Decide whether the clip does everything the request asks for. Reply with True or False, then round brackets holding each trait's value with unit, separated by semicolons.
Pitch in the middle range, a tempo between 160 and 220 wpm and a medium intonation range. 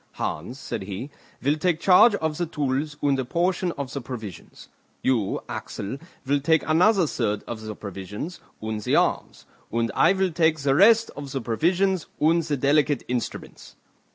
False (145 Hz; 170 wpm; 5.9 semitones)